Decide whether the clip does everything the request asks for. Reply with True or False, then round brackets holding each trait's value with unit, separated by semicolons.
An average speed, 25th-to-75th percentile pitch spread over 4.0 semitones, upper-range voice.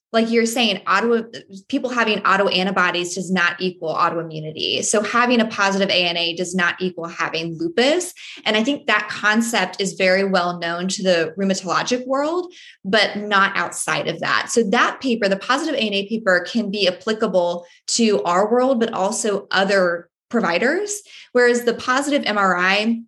True (160 wpm; 4.4 semitones; 200 Hz)